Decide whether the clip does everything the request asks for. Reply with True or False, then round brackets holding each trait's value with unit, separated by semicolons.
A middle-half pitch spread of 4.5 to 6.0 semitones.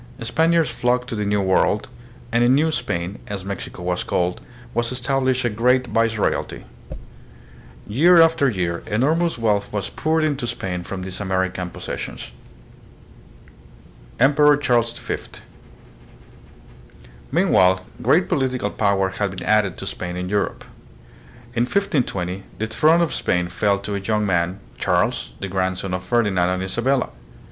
True (5.3 semitones)